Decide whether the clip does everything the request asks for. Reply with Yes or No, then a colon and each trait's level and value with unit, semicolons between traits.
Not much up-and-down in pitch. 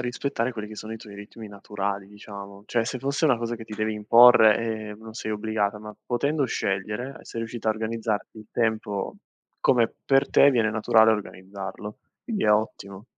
Yes: narrow, 2.2 semitones